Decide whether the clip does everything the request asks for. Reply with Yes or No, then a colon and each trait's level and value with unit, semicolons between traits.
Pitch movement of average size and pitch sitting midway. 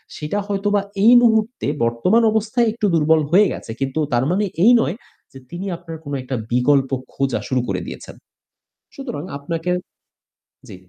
No: wide, 7.4 semitones; medium, 170 Hz